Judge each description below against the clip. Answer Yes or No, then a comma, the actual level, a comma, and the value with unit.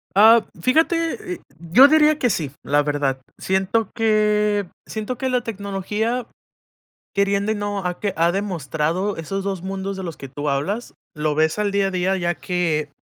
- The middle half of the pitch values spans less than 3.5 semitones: No, average, 4.2 semitones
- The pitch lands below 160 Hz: No, high, 195 Hz